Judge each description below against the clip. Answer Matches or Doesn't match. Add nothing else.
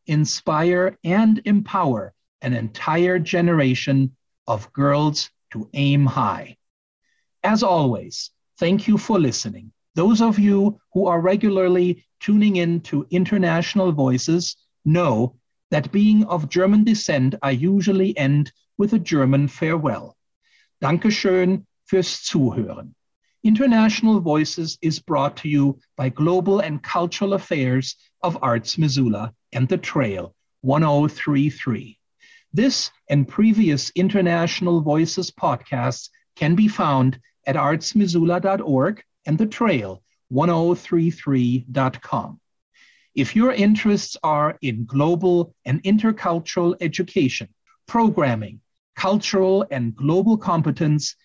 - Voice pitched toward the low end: Doesn't match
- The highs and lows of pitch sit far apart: Matches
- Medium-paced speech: Doesn't match